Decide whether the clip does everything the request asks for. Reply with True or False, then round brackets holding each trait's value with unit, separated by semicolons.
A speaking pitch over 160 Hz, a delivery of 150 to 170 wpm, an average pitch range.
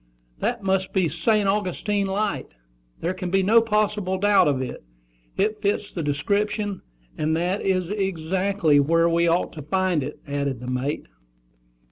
True (185 Hz; 160 wpm; 4.3 semitones)